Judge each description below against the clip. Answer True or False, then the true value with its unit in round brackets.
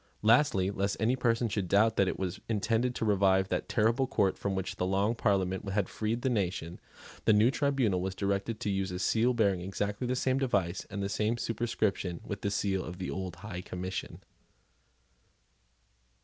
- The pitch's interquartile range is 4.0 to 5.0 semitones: False (3.2 semitones)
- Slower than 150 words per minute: False (185 wpm)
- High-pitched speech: False (100 Hz)